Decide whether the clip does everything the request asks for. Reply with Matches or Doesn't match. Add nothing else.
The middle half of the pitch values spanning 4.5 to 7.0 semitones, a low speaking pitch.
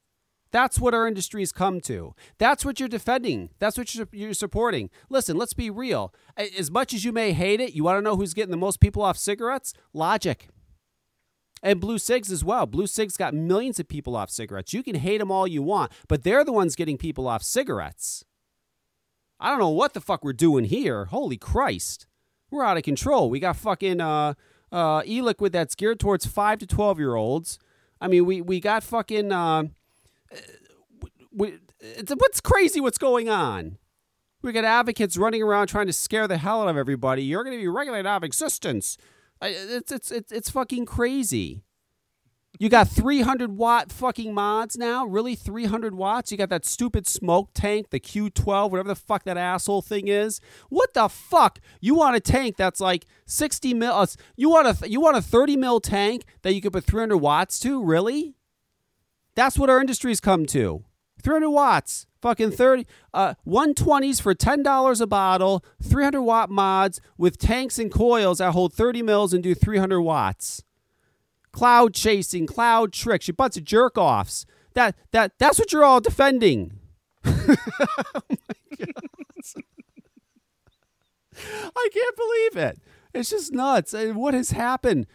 Doesn't match